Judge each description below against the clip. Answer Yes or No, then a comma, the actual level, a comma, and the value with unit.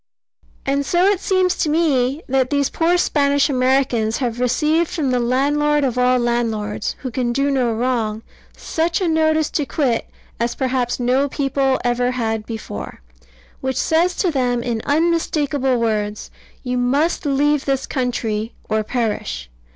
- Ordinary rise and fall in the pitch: Yes, average, 3.6 semitones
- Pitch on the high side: Yes, very high, 260 Hz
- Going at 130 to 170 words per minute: Yes, average, 150 wpm